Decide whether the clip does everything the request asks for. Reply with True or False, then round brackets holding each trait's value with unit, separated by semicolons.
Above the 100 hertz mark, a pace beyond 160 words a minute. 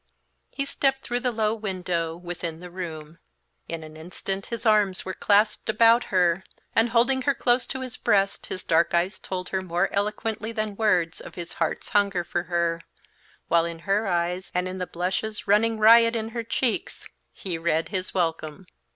True (190 Hz; 180 wpm)